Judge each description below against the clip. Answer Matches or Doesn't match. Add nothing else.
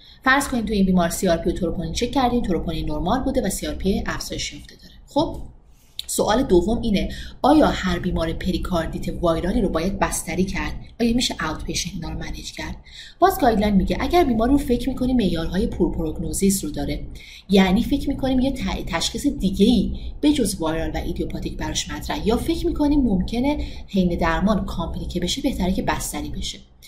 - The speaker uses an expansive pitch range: Matches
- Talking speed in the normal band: Doesn't match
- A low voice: Doesn't match